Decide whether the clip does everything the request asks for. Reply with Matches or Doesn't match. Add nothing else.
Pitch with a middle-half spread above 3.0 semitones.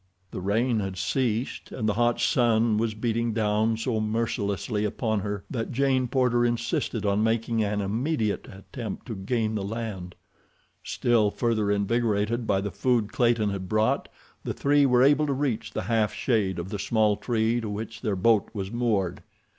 Doesn't match